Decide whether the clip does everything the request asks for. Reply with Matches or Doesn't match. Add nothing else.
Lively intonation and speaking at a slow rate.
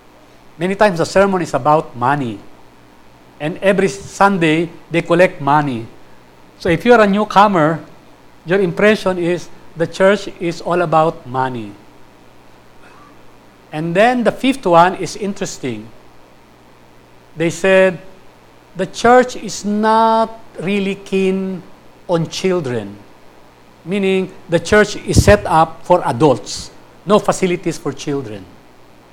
Matches